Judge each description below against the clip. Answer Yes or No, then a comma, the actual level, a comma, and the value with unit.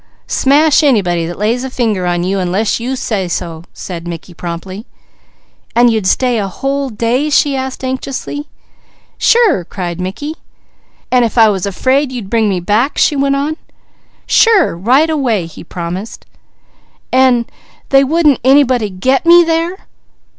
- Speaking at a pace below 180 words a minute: Yes, average, 150 wpm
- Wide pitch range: Yes, wide, 6.7 semitones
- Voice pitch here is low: No, high, 240 Hz